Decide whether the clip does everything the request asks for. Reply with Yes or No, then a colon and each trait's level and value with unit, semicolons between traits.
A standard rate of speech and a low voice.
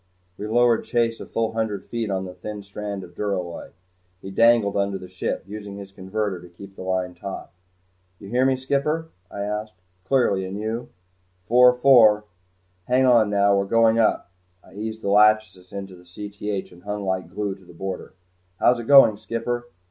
Yes: average, 180 wpm; low, 105 Hz